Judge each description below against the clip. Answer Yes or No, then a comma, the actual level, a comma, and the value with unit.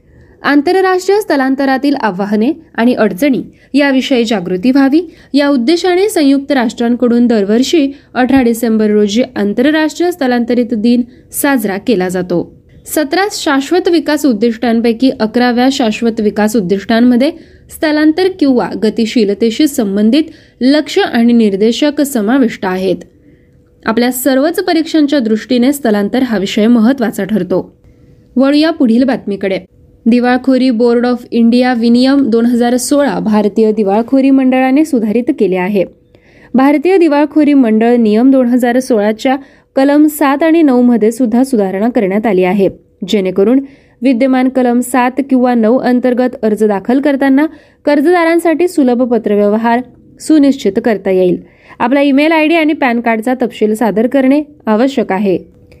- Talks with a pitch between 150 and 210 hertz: No, very high, 250 Hz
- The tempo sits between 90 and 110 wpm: No, average, 120 wpm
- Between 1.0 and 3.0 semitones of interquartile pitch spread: No, average, 4.2 semitones